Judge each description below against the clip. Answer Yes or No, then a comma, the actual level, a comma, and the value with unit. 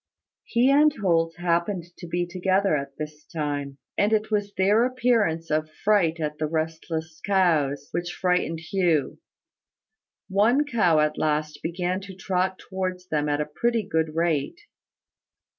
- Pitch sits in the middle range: Yes, medium, 175 Hz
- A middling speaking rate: Yes, average, 145 wpm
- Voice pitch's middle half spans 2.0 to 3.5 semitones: No, average, 4.1 semitones